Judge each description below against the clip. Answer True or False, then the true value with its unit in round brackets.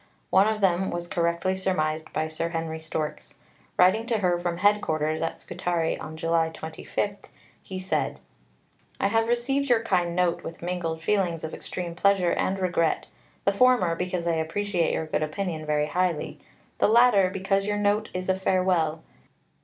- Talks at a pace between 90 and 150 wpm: False (165 wpm)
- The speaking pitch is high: False (180 Hz)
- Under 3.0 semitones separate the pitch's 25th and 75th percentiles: False (3.4 semitones)